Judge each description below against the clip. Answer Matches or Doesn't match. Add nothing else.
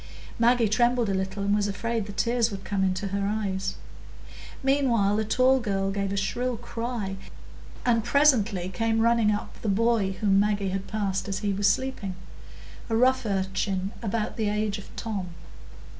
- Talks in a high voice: Matches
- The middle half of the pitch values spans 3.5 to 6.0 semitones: Doesn't match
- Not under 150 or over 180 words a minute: Matches